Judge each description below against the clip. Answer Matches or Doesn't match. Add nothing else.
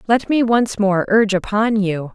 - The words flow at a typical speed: Matches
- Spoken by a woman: Matches